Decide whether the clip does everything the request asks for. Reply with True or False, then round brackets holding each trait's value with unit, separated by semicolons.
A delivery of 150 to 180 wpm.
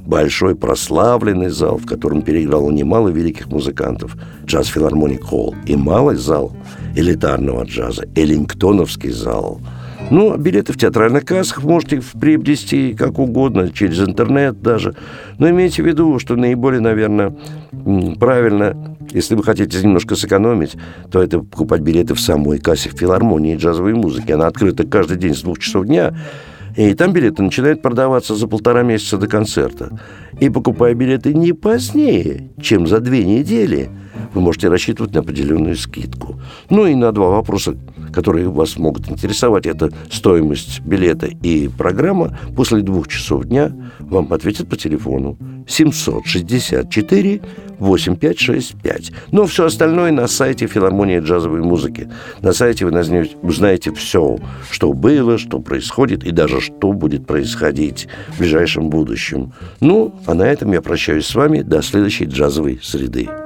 False (140 wpm)